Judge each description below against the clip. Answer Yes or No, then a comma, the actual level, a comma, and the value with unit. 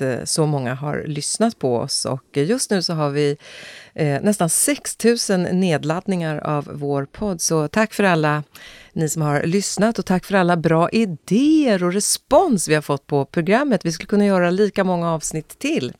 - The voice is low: No, medium, 175 Hz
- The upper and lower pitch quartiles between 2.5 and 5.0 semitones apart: No, wide, 5.5 semitones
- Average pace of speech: Yes, average, 175 wpm